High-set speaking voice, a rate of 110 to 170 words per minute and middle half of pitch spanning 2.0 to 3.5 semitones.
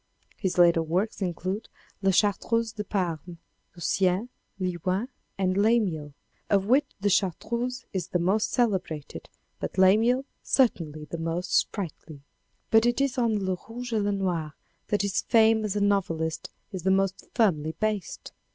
No: high, 195 Hz; average, 150 wpm; average, 3.9 semitones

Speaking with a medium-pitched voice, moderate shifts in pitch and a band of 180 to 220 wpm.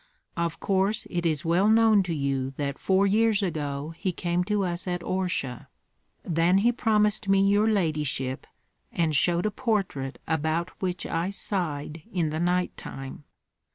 No: medium, 175 Hz; average, 4.2 semitones; average, 155 wpm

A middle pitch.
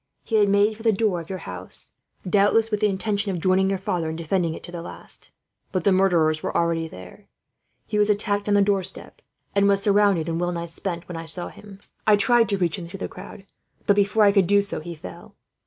No: high, 195 Hz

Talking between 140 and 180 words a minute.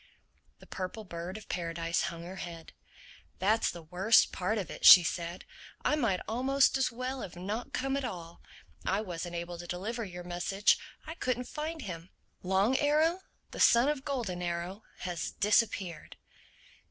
Yes: average, 165 wpm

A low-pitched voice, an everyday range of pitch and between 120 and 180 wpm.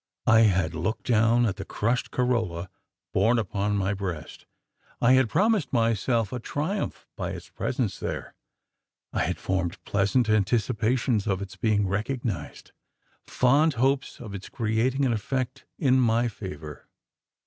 Yes: low, 115 Hz; average, 4.1 semitones; average, 140 wpm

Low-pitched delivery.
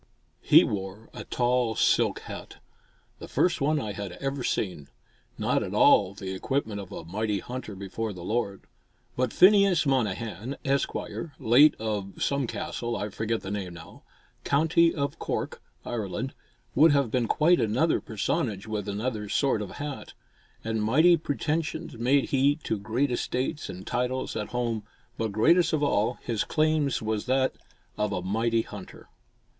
Yes: low, 115 Hz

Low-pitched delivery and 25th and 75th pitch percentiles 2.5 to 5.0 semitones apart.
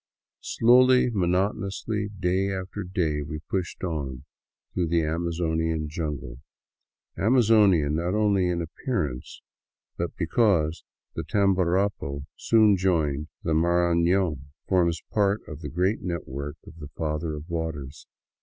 Yes: very low, 85 Hz; average, 4.0 semitones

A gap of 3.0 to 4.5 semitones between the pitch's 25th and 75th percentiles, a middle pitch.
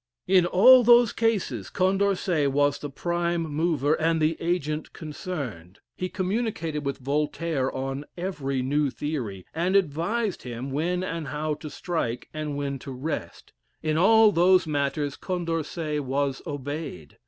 Yes: average, 4.1 semitones; medium, 155 Hz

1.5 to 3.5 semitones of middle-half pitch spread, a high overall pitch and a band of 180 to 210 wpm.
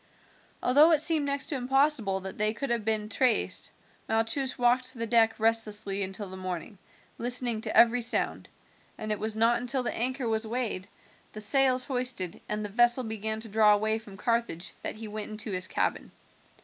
Yes: average, 2.9 semitones; high, 225 Hz; average, 185 wpm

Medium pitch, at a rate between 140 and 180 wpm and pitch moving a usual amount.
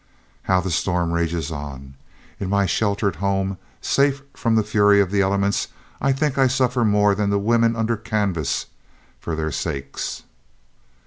No: low, 100 Hz; average, 155 wpm; average, 4.5 semitones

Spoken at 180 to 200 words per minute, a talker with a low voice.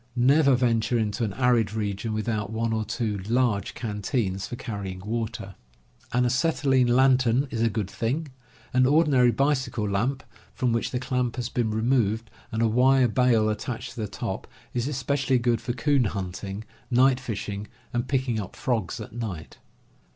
No: average, 165 wpm; low, 120 Hz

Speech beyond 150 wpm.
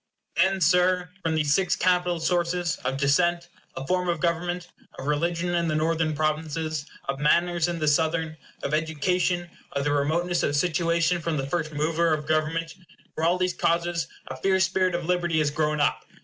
Yes: average, 180 wpm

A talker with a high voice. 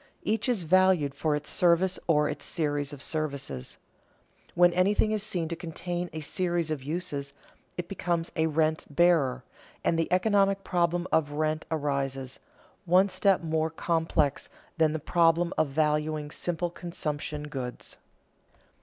No: medium, 160 Hz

